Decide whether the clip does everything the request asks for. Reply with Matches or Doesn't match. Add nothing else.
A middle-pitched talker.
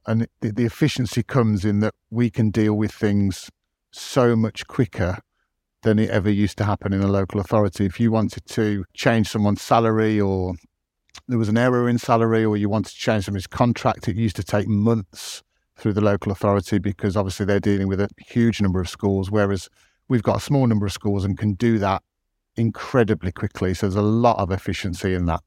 Doesn't match